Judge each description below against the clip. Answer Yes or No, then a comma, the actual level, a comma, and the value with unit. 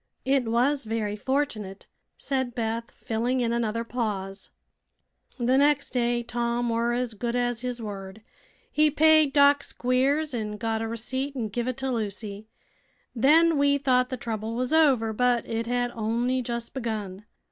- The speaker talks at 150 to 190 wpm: Yes, average, 160 wpm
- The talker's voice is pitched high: Yes, high, 240 Hz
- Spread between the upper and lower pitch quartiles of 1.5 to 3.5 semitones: Yes, average, 2.7 semitones